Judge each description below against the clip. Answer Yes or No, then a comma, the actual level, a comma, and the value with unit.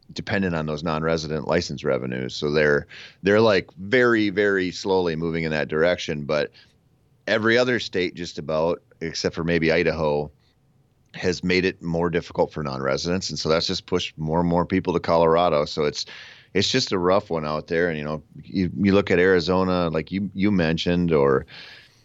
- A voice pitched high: No, very low, 85 Hz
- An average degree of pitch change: Yes, average, 3.3 semitones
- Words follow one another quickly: No, average, 180 wpm